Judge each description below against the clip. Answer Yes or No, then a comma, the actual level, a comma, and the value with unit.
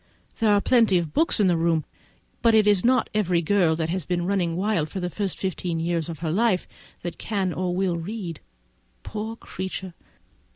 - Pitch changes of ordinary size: Yes, average, 3.6 semitones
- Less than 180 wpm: Yes, average, 170 wpm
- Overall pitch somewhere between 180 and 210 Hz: Yes, medium, 185 Hz